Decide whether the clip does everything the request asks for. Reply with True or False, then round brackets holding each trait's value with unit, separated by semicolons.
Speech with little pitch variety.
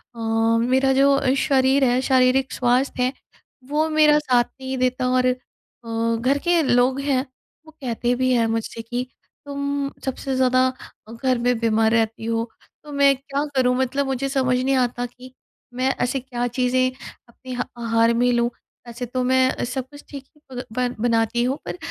True (1.8 semitones)